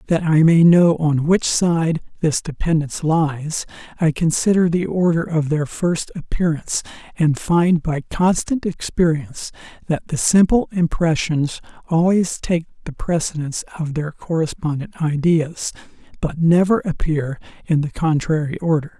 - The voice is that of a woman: No, male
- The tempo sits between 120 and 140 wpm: Yes, slow, 135 wpm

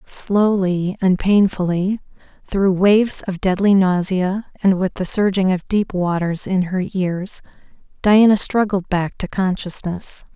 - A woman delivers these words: Yes, female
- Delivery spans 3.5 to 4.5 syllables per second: Yes, 4.0 syllables/s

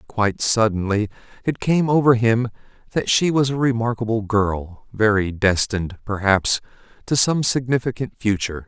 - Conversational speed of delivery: No, slow, 120 wpm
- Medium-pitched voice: No, low, 110 Hz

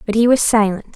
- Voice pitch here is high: Yes, high, 220 Hz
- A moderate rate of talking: No, fast, 250 wpm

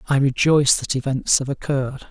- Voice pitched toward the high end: No, low, 135 Hz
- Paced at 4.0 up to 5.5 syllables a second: No, 5.7 syllables/s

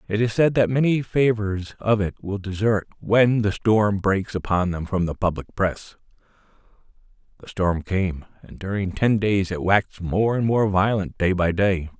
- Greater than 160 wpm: Yes, average, 180 wpm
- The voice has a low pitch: Yes, low, 100 Hz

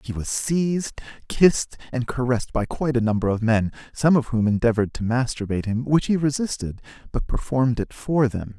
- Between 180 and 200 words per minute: Yes, average, 190 wpm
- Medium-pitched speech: No, low, 125 Hz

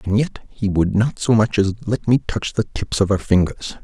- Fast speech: Yes, fast, 250 wpm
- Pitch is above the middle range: No, low, 105 Hz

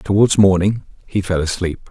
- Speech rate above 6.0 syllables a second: No, 4.8 syllables/s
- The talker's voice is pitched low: Yes, very low, 95 Hz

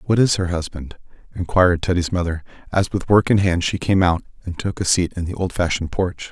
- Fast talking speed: Yes, fast, 220 wpm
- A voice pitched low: Yes, very low, 90 Hz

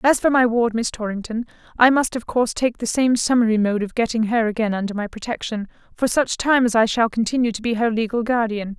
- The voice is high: Yes, high, 230 Hz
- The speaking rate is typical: No, fast, 230 wpm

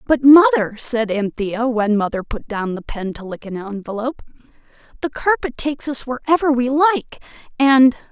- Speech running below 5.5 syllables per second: Yes, 5.0 syllables/s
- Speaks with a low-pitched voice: No, very high, 250 Hz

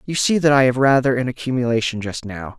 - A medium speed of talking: No, fast, 230 wpm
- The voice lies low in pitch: Yes, low, 130 Hz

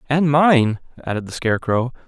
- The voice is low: Yes, low, 130 Hz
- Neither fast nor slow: Yes, average, 145 wpm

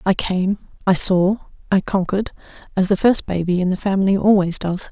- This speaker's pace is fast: No, average, 185 wpm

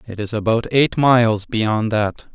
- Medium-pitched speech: No, low, 115 Hz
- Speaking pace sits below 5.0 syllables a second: Yes, 4.2 syllables/s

